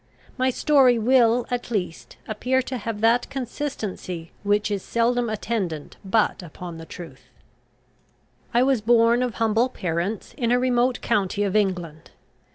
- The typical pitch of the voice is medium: No, high, 225 Hz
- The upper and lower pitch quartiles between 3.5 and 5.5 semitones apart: Yes, average, 4.0 semitones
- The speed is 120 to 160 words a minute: Yes, average, 140 wpm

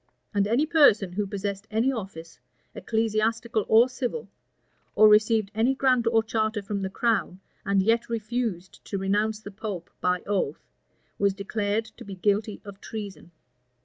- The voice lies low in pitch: No, high, 215 Hz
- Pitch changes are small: Yes, narrow, 2.3 semitones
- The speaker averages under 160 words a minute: Yes, average, 150 wpm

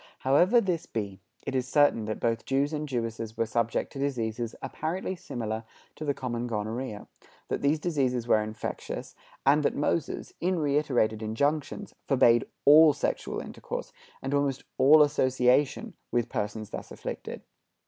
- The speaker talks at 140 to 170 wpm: Yes, average, 150 wpm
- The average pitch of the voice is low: Yes, low, 130 Hz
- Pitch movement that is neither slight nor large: Yes, average, 4.4 semitones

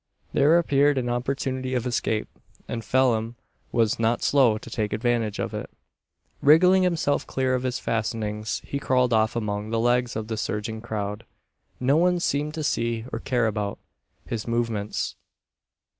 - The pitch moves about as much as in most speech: Yes, average, 3.2 semitones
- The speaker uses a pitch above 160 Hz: No, low, 120 Hz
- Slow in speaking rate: No, average, 160 wpm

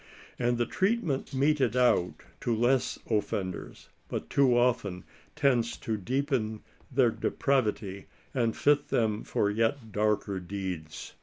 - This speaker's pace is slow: Yes, slow, 125 wpm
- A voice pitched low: Yes, low, 115 Hz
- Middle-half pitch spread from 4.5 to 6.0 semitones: No, average, 4.1 semitones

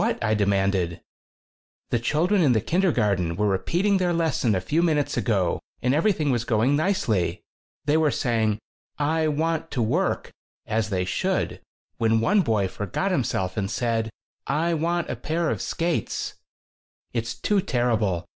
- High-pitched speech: No, low, 120 Hz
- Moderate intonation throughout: No, wide, 7.7 semitones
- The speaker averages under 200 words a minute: Yes, average, 155 wpm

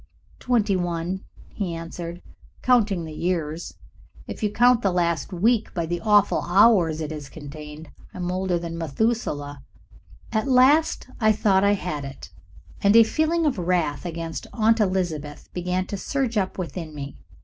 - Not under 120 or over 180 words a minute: Yes, average, 160 wpm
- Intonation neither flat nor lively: Yes, average, 4.8 semitones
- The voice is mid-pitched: Yes, medium, 180 Hz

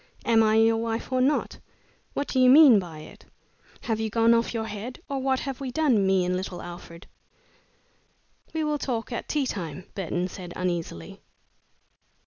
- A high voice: Yes, high, 225 Hz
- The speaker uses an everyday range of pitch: No, wide, 5.9 semitones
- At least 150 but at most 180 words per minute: Yes, average, 175 wpm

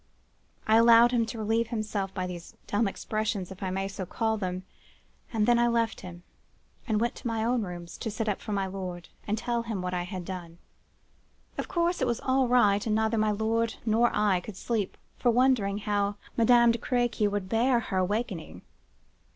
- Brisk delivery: No, average, 195 wpm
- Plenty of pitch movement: No, average, 3.3 semitones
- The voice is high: Yes, high, 215 Hz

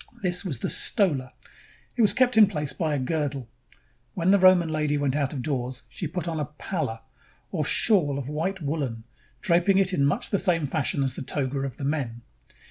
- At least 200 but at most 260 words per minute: Yes, fast, 205 wpm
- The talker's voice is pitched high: No, medium, 150 Hz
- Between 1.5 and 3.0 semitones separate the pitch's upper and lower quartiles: No, average, 4.8 semitones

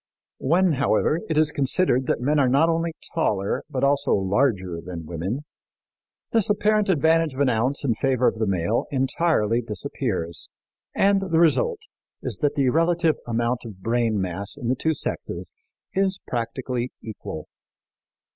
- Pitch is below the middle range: Yes, low, 130 Hz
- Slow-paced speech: No, average, 155 wpm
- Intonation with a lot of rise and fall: Yes, wide, 6.4 semitones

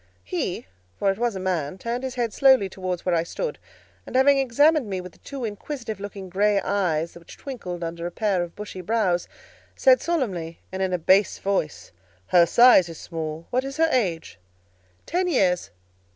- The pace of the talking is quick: No, average, 185 wpm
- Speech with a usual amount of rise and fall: No, wide, 6.2 semitones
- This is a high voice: Yes, high, 195 Hz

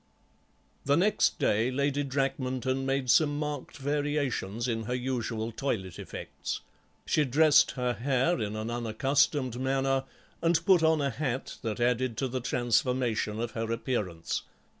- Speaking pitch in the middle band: No, low, 130 Hz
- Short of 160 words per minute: Yes, average, 140 wpm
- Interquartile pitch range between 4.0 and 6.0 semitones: No, average, 3.3 semitones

